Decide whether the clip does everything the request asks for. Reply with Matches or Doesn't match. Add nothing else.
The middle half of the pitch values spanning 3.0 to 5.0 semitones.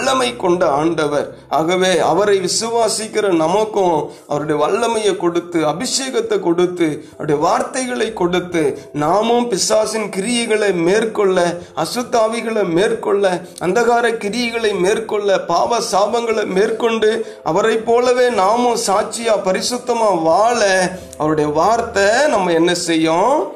Matches